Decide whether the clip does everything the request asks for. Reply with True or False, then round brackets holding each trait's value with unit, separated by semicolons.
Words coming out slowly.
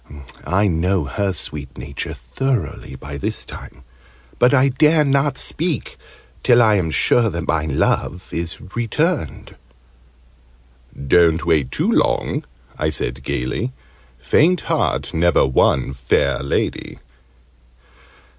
True (115 wpm)